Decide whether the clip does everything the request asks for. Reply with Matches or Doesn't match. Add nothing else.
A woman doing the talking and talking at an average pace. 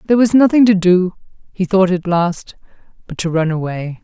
Matches